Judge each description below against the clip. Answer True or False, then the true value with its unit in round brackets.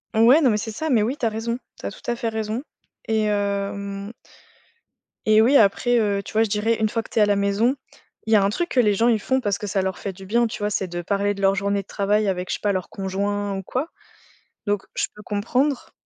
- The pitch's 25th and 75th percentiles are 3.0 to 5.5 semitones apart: False (2.4 semitones)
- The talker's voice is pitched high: True (210 Hz)